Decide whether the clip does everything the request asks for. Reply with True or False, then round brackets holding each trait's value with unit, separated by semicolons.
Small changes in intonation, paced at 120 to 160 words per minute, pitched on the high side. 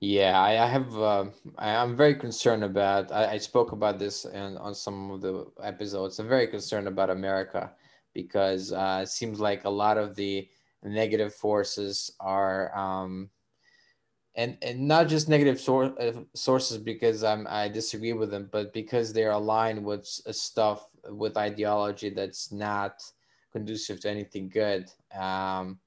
False (2.1 semitones; 145 wpm; 105 Hz)